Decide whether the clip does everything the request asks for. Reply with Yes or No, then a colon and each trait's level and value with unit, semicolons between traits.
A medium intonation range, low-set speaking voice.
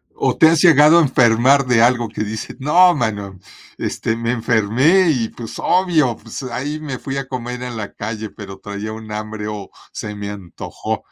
Yes: average, 4.4 semitones; low, 120 Hz